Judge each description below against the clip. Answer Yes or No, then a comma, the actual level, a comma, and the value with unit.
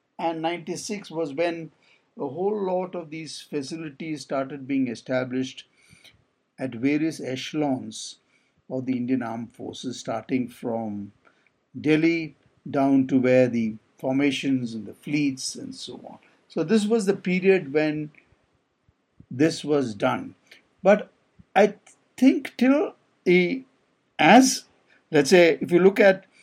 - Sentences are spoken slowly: Yes, slow, 125 wpm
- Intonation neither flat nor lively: No, wide, 5.8 semitones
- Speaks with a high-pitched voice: No, medium, 155 Hz